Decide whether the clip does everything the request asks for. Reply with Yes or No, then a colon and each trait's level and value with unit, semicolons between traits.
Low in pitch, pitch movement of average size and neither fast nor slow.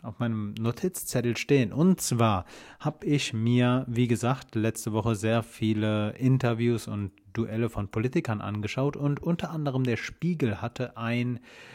Yes: low, 120 Hz; average, 3.0 semitones; average, 145 wpm